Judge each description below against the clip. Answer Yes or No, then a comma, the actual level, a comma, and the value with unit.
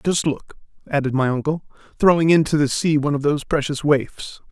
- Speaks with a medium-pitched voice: Yes, medium, 145 Hz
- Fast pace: No, average, 185 wpm